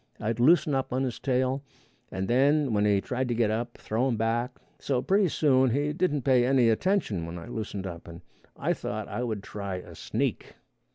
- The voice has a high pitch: No, low, 120 Hz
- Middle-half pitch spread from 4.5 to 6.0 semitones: No, average, 4.0 semitones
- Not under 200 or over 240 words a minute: Yes, fast, 205 wpm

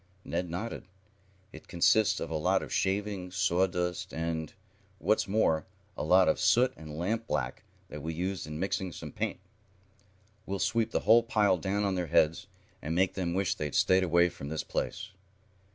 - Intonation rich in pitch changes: No, average, 3.2 semitones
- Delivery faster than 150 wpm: Yes, average, 170 wpm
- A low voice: Yes, very low, 90 Hz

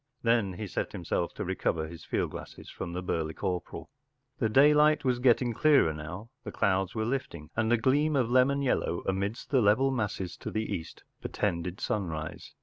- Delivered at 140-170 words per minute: No, average, 180 wpm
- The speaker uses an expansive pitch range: Yes, wide, 6.4 semitones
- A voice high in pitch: No, low, 105 Hz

